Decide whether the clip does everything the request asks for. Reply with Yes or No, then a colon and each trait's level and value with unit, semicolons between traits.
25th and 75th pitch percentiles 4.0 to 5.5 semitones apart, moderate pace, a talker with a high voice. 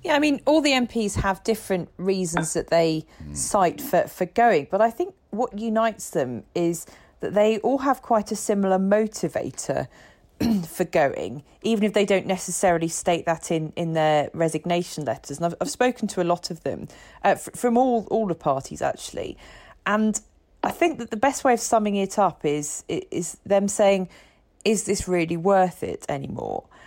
Yes: average, 4.9 semitones; average, 185 wpm; high, 195 Hz